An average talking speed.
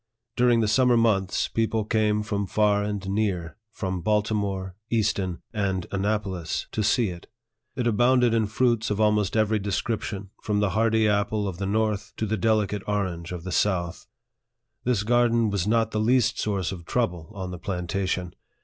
Yes: average, 165 wpm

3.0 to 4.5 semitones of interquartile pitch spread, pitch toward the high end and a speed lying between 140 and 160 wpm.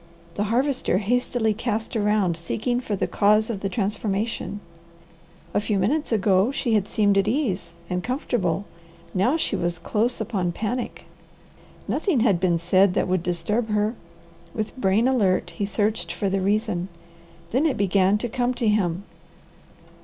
Yes: average, 3.7 semitones; high, 210 Hz; average, 155 wpm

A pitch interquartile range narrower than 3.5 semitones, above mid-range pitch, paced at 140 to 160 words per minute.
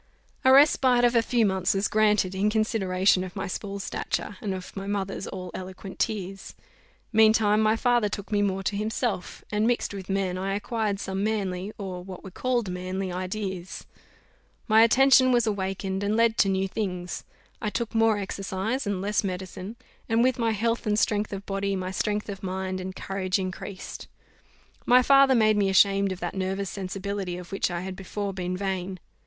No: narrow, 2.4 semitones; high, 200 Hz; average, 185 wpm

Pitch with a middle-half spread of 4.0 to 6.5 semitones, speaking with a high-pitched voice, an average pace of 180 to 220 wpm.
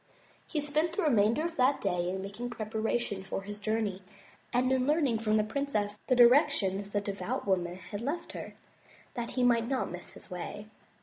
Yes: average, 4.5 semitones; high, 225 Hz; average, 185 wpm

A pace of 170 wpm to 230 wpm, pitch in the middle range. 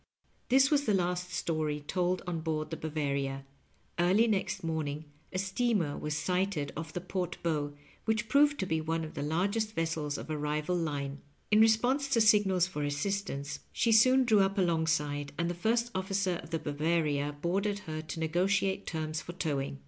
Yes: average, 180 wpm; medium, 170 Hz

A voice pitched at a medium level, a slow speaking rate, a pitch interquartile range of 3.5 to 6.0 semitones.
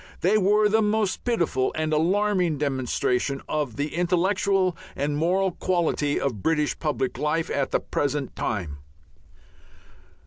Yes: medium, 160 Hz; slow, 130 wpm; average, 4.9 semitones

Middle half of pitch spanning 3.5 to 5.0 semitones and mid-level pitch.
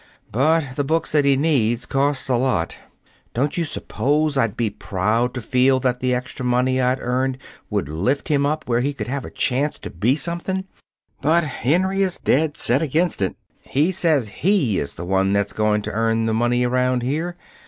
No: average, 4.2 semitones; low, 130 Hz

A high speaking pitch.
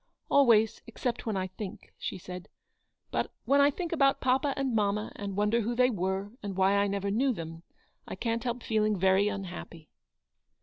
Yes: high, 210 Hz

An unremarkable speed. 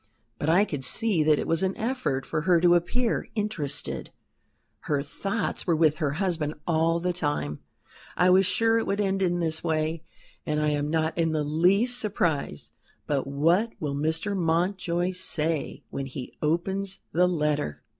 Yes: average, 170 wpm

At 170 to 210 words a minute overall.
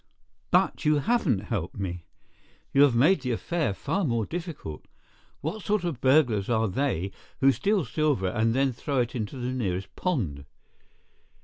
No: average, 155 wpm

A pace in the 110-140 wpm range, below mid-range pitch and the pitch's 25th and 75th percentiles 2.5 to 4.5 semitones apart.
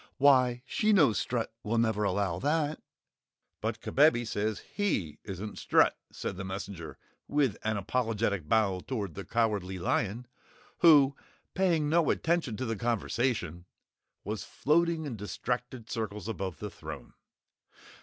No: slow, 135 wpm; low, 115 Hz; wide, 5.5 semitones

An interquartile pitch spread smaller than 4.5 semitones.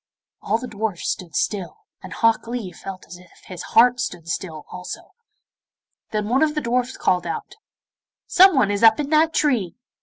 No: wide, 5.6 semitones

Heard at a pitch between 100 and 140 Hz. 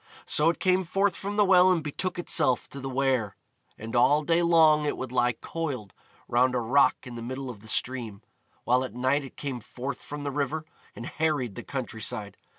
Yes: low, 135 Hz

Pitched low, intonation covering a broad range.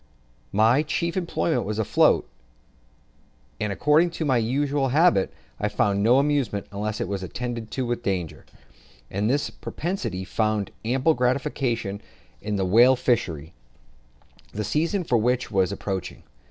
Yes: low, 120 Hz; wide, 5.8 semitones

